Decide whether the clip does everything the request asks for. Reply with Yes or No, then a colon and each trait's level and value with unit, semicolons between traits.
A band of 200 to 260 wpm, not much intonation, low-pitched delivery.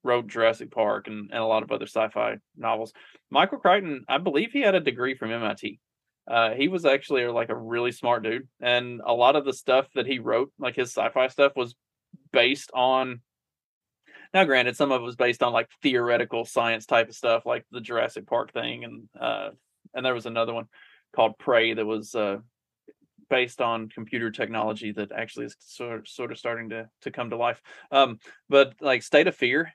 Yes: fast, 205 wpm; narrow, 2.1 semitones; low, 120 Hz